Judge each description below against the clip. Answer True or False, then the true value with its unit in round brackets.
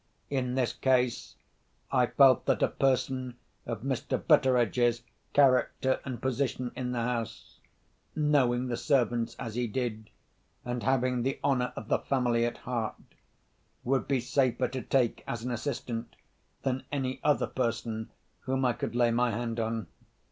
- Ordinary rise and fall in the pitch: False (1.9 semitones)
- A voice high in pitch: False (125 Hz)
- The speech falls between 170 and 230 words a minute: False (145 wpm)